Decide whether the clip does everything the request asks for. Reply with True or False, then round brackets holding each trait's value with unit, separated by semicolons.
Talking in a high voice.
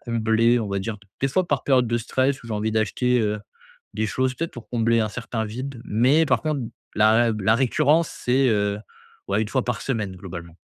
False (115 Hz)